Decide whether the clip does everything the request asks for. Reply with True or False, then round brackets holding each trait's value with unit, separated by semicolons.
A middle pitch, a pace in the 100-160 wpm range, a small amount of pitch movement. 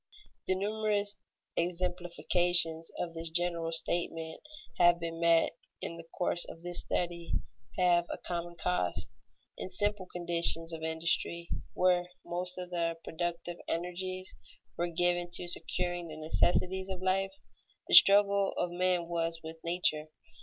True (175 Hz; 140 wpm; 1.5 semitones)